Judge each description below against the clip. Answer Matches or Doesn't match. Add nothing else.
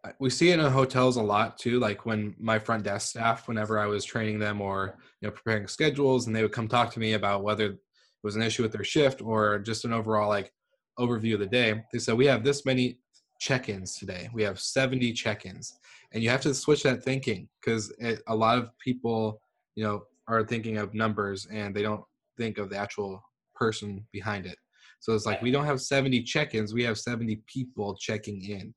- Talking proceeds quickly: Matches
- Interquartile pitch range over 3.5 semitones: Doesn't match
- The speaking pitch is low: Matches